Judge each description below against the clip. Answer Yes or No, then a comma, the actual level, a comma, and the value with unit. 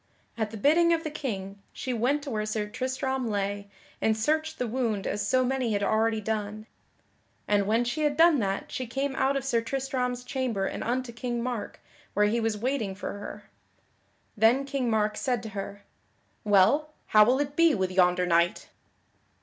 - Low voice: No, high, 235 Hz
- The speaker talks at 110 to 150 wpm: No, average, 185 wpm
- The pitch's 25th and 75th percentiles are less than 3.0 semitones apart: No, average, 4.3 semitones